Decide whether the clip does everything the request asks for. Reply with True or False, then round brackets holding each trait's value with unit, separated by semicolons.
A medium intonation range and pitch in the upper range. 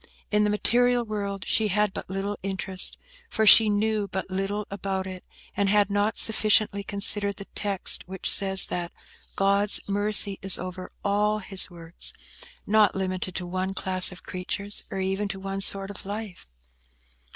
False (1.6 semitones; 200 Hz)